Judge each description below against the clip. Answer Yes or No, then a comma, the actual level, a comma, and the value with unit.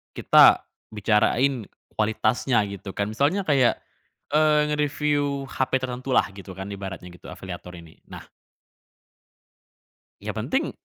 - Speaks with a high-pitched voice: No, low, 120 Hz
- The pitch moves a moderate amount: No, wide, 6.3 semitones